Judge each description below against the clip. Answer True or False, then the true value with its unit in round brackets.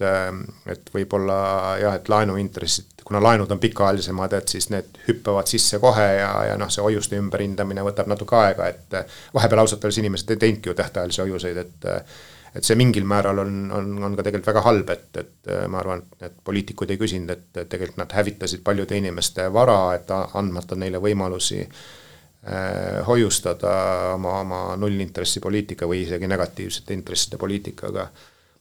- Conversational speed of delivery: True (155 wpm)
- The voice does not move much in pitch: True (2.0 semitones)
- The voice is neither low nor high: False (100 Hz)